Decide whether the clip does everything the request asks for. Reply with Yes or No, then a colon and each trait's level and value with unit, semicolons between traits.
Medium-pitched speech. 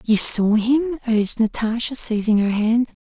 No: high, 230 Hz